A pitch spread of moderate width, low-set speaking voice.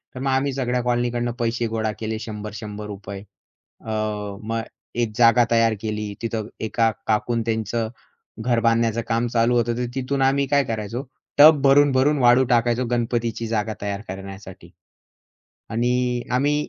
No: narrow, 2.2 semitones; low, 115 Hz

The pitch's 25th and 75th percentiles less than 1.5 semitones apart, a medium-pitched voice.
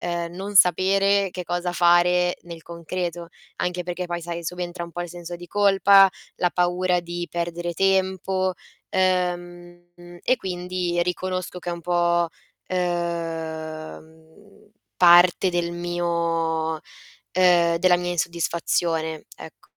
Yes: narrow, 1.0 semitones; medium, 175 Hz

